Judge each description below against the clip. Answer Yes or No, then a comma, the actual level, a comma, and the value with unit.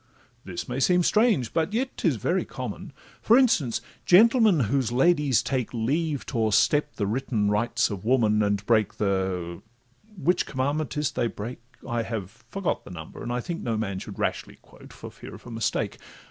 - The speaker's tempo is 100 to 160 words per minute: No, average, 175 wpm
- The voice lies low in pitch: Yes, low, 120 Hz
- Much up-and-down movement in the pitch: Yes, wide, 6.3 semitones